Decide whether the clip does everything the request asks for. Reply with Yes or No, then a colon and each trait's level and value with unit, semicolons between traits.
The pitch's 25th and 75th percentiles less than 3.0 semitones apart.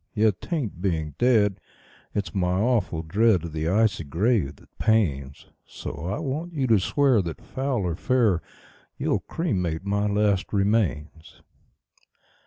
No: wide, 5.4 semitones